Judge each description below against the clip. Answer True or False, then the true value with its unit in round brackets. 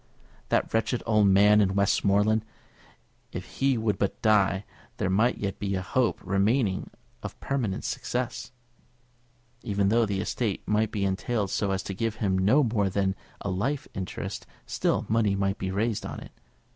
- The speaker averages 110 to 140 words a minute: False (165 wpm)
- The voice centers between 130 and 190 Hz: False (105 Hz)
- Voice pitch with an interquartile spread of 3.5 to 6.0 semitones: False (2.6 semitones)